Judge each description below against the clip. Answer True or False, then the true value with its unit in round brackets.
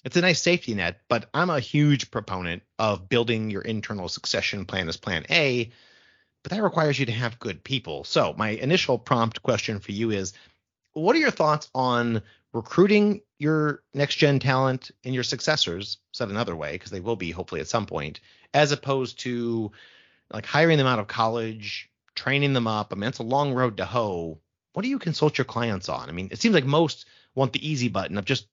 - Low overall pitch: True (120 Hz)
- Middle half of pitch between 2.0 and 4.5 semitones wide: False (5.4 semitones)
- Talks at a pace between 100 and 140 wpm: False (205 wpm)